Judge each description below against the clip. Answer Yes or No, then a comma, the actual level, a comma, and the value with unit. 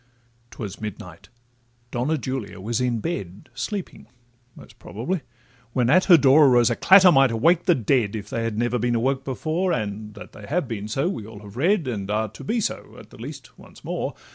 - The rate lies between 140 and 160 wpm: No, average, 190 wpm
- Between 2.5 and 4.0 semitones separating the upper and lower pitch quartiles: No, average, 4.5 semitones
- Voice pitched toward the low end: Yes, low, 120 Hz